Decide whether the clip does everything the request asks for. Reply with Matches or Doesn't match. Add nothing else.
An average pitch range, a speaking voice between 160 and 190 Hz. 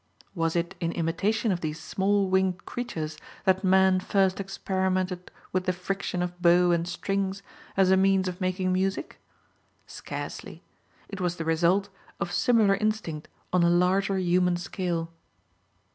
Doesn't match